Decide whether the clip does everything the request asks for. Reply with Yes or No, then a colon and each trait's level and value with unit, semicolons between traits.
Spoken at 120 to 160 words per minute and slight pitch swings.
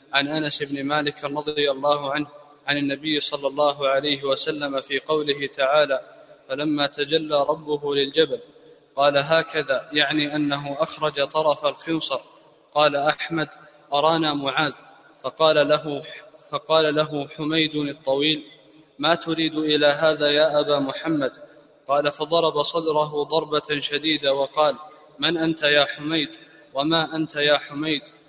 Yes: average, 125 wpm; narrow, 1.3 semitones